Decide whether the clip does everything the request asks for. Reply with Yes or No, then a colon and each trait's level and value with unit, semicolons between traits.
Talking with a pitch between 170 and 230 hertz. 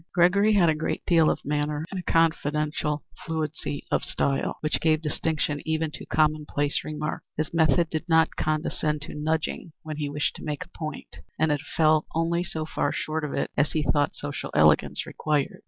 No: medium, 155 Hz